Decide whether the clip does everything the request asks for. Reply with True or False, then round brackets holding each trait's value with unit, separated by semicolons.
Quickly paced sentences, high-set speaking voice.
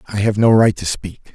False (265 wpm; 105 Hz)